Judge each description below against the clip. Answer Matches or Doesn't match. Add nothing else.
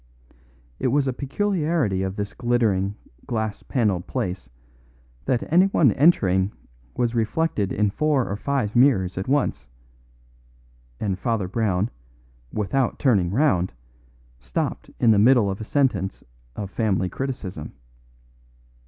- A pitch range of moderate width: Doesn't match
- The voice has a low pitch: Matches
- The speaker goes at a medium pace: Doesn't match